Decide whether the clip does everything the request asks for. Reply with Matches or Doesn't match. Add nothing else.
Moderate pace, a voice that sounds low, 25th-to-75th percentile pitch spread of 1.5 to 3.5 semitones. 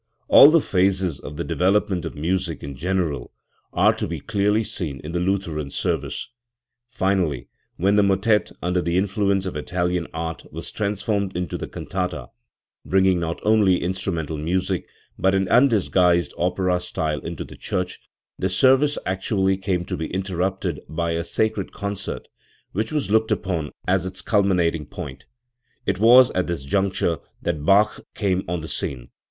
Matches